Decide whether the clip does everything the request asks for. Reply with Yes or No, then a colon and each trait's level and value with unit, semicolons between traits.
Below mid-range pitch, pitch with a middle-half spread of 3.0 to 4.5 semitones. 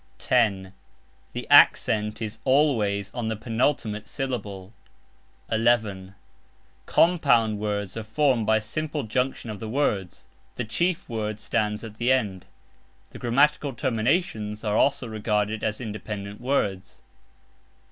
Yes: low, 110 Hz; average, 3.3 semitones